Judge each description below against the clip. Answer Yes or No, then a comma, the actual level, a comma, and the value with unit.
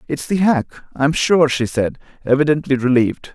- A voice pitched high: No, medium, 140 Hz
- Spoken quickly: No, average, 180 wpm